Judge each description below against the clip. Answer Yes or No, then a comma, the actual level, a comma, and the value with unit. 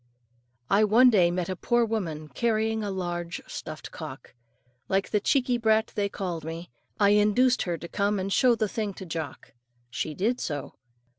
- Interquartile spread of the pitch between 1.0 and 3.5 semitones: No, average, 4.3 semitones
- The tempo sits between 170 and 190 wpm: Yes, average, 175 wpm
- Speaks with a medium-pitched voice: No, high, 200 Hz